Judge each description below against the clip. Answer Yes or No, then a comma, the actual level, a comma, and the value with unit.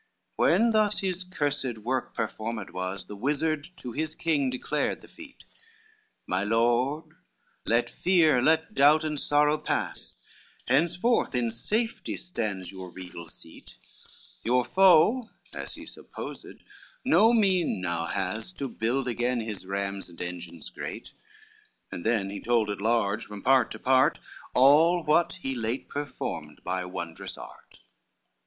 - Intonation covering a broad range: Yes, wide, 7.6 semitones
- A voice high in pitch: No, low, 125 Hz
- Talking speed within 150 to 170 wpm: No, average, 140 wpm